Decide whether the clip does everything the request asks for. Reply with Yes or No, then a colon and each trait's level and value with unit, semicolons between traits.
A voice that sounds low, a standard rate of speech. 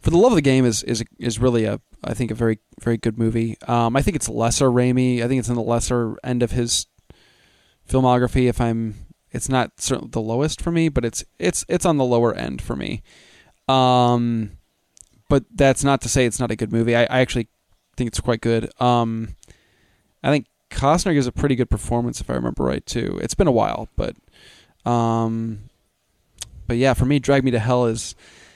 No: low, 120 Hz; fast, 210 wpm